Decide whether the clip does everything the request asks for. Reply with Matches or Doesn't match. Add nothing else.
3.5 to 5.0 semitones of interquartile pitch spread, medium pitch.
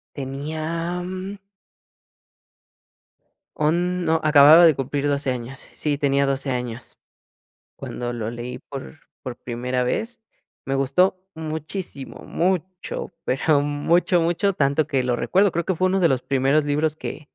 Matches